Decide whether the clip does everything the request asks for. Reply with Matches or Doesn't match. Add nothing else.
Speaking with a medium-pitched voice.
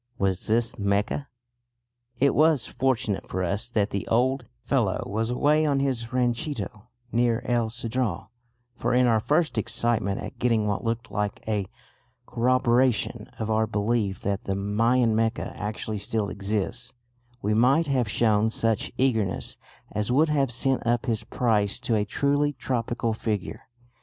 Doesn't match